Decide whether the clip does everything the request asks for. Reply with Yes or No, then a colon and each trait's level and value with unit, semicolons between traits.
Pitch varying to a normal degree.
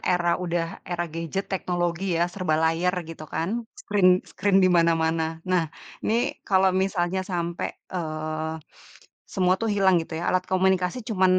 No: narrow, 2.2 semitones